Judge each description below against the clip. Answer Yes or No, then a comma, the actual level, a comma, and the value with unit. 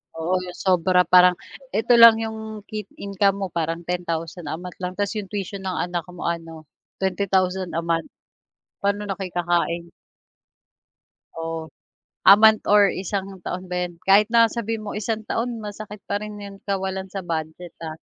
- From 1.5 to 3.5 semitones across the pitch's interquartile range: Yes, average, 2.8 semitones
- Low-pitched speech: No, high, 190 Hz